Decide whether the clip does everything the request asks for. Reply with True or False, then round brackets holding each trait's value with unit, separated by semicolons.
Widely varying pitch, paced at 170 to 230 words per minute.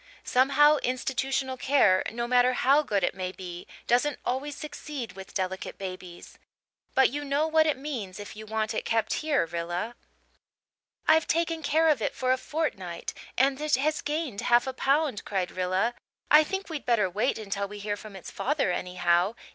True (6.9 semitones; 180 wpm)